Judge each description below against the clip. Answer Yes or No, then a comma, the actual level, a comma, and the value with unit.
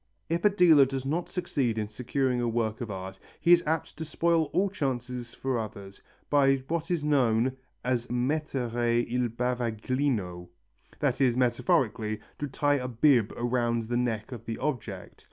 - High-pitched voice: No, low, 125 Hz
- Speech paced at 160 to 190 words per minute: Yes, average, 165 wpm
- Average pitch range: Yes, average, 3.8 semitones